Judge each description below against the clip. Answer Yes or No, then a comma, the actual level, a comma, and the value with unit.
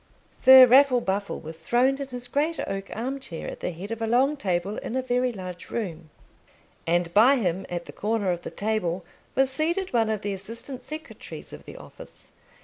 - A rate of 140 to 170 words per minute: No, average, 200 wpm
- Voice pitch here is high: Yes, high, 225 Hz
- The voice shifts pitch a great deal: Yes, wide, 5.9 semitones